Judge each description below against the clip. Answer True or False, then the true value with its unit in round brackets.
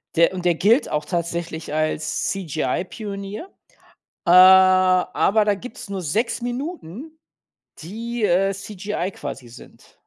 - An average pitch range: True (4.0 semitones)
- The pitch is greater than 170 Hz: True (190 Hz)